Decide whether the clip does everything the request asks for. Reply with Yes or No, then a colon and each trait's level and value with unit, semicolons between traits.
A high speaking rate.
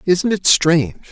No: average, 160 wpm